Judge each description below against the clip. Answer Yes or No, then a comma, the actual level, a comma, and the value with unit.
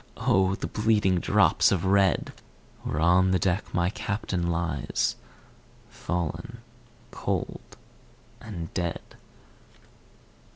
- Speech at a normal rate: No, slow, 95 wpm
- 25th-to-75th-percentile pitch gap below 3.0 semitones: Yes, narrow, 2.4 semitones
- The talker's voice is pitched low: Yes, very low, 95 Hz